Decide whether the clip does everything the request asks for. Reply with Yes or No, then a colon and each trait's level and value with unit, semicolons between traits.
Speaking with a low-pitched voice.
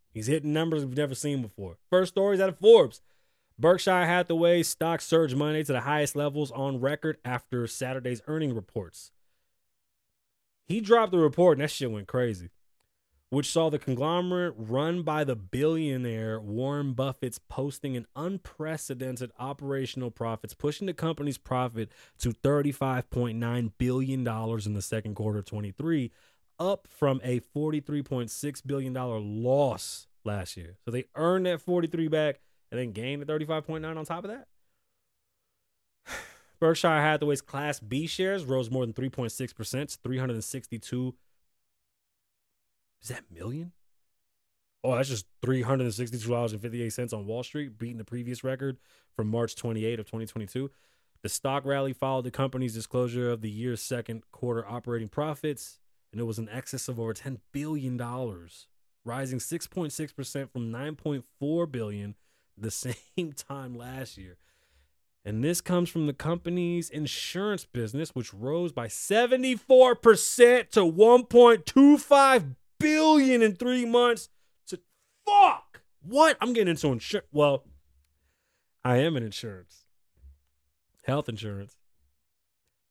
Yes: low, 130 Hz